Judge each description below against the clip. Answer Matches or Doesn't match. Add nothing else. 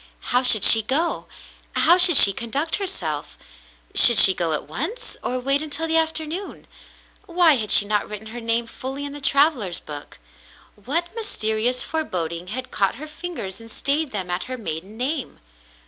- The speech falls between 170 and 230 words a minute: Matches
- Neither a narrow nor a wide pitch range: Doesn't match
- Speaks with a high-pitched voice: Matches